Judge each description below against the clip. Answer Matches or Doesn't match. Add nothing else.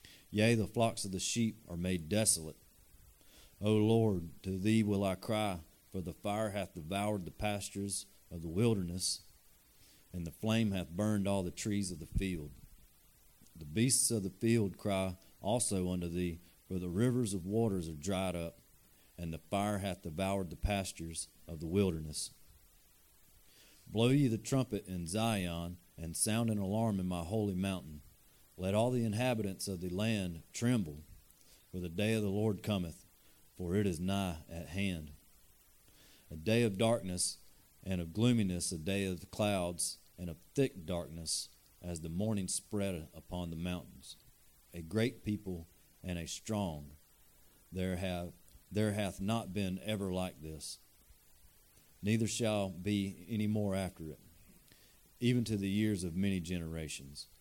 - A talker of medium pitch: Doesn't match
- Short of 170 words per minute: Matches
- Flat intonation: Doesn't match